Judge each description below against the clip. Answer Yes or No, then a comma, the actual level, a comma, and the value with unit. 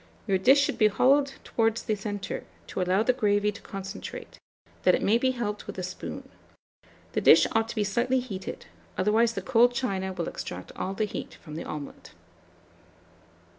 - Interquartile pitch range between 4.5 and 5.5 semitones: No, average, 3.7 semitones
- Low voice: No, high, 210 Hz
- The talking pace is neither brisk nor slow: Yes, average, 180 wpm